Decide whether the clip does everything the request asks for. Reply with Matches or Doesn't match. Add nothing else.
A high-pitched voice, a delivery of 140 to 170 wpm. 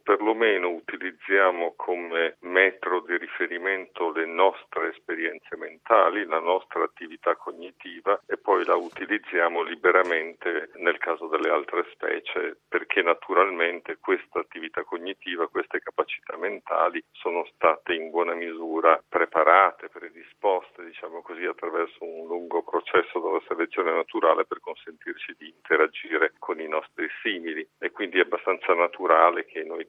Doesn't match